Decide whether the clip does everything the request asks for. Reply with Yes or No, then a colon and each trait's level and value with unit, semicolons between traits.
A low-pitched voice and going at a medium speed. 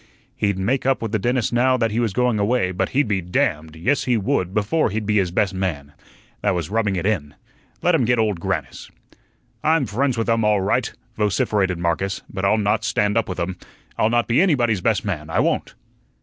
No: low, 105 Hz; fast, 215 wpm